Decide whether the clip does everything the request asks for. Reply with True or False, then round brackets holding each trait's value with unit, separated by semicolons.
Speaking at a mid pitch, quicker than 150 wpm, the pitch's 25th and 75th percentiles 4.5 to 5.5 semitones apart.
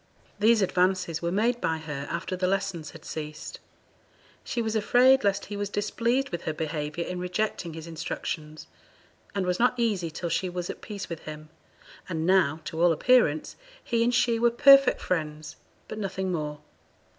True (180 Hz; 175 wpm; 5.2 semitones)